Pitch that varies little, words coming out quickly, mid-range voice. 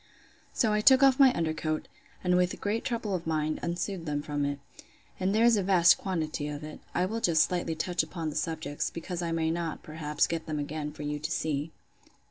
No: average, 3.2 semitones; fast, 220 wpm; medium, 165 Hz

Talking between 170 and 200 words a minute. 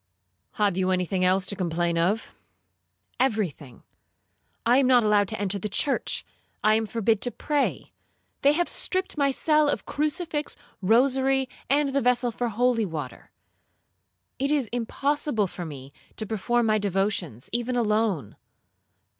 No: average, 140 wpm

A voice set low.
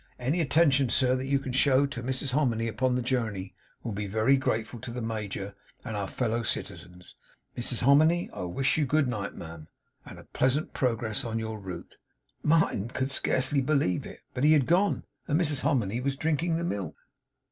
Yes: low, 125 Hz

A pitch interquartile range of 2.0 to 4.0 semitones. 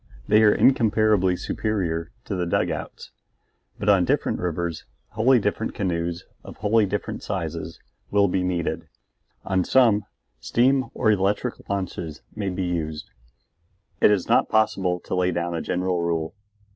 Yes: average, 3.5 semitones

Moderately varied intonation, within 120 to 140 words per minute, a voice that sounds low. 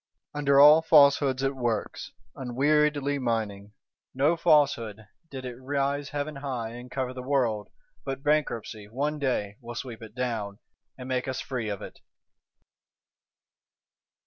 Yes: average, 3.6 semitones; slow, 135 wpm; low, 130 Hz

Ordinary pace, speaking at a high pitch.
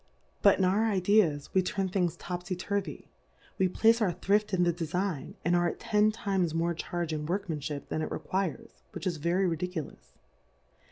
No: average, 175 wpm; medium, 180 Hz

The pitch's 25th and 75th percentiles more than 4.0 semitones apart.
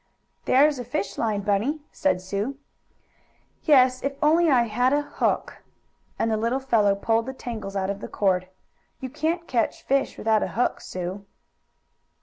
Yes: average, 5.1 semitones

